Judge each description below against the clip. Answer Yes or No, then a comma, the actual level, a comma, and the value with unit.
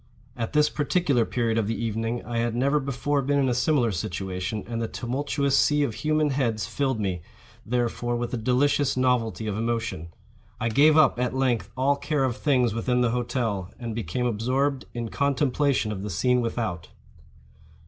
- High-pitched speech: No, low, 120 Hz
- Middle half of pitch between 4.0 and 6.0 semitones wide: No, average, 3.5 semitones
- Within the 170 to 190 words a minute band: Yes, average, 180 wpm